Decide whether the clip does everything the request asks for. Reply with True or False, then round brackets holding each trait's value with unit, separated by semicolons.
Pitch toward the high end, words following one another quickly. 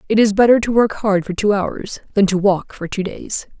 True (205 Hz; 250 wpm)